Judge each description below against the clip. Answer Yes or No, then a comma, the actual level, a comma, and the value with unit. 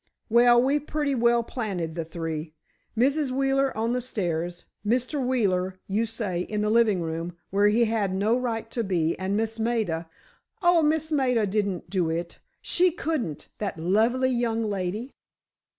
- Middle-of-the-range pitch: No, high, 220 Hz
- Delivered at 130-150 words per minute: No, average, 160 wpm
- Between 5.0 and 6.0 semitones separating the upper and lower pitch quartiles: Yes, average, 5.3 semitones